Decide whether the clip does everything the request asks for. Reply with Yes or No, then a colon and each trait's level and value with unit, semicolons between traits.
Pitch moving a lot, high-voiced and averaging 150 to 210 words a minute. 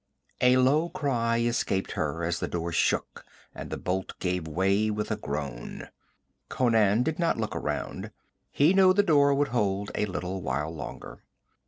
No: wide, 7.1 semitones; low, 105 Hz; average, 165 wpm